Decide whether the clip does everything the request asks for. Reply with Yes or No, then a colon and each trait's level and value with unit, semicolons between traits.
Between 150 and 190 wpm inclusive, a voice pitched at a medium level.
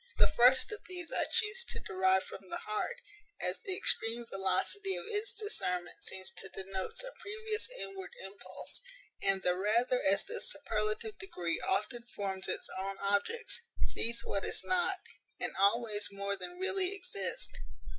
No: average, 155 wpm; high, 230 Hz